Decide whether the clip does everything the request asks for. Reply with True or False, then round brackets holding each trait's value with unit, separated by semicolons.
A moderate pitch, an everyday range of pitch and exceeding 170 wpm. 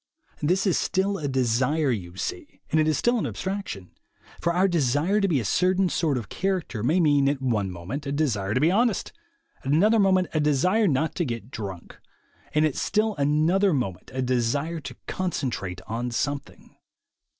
False (150 Hz; 6.8 semitones; 185 wpm)